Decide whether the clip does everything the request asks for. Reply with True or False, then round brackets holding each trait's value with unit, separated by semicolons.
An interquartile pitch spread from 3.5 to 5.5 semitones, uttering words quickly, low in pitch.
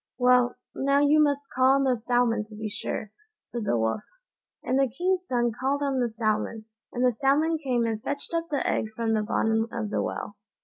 False (3.8 semitones; 210 wpm; 245 Hz)